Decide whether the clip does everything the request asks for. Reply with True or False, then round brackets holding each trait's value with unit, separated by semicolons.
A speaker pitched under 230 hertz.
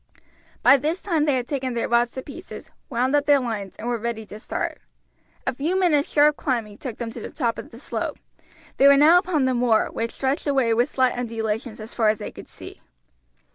False (255 Hz)